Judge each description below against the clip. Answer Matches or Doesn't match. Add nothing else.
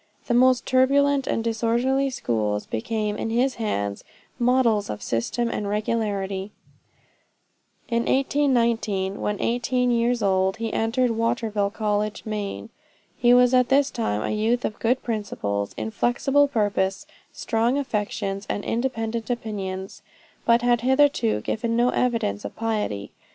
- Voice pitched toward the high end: Matches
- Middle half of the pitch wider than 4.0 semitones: Doesn't match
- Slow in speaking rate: Matches